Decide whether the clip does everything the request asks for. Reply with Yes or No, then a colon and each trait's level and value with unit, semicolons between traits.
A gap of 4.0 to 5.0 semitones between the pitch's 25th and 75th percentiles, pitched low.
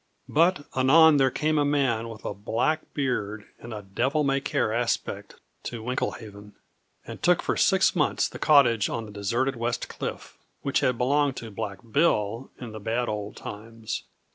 Yes: average, 4.3 semitones; low, 120 Hz